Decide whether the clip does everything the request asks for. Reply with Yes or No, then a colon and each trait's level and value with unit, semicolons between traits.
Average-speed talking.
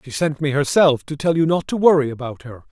No: fast, 265 wpm